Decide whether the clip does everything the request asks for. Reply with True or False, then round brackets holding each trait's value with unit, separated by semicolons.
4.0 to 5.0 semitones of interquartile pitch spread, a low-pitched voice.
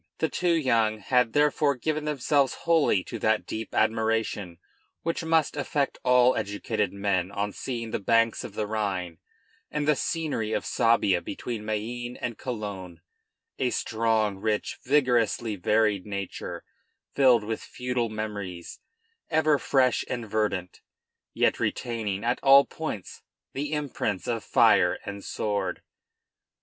True (4.3 semitones; 115 Hz)